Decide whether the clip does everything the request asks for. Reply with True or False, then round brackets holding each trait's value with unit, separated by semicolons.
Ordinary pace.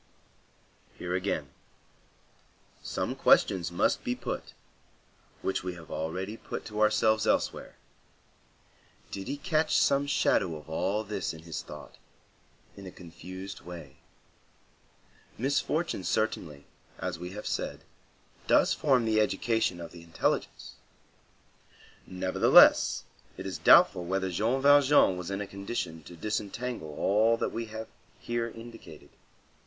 False (125 wpm)